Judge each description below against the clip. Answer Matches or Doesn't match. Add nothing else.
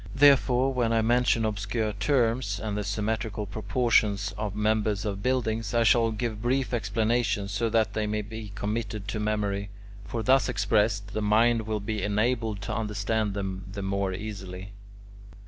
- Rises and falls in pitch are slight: Matches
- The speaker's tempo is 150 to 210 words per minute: Matches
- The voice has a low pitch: Matches